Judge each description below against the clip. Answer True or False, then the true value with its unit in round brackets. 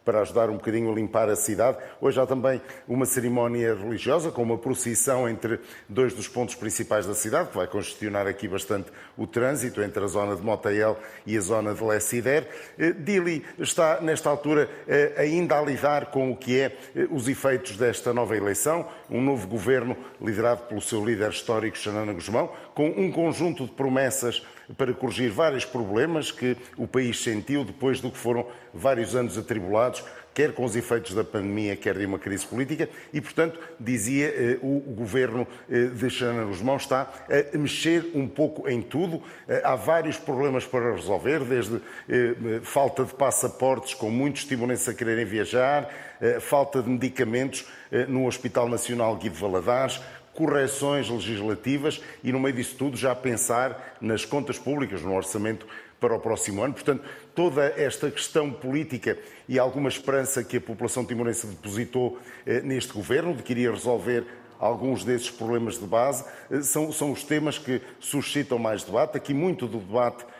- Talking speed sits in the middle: True (170 wpm)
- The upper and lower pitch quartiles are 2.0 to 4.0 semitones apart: True (3.1 semitones)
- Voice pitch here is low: True (125 Hz)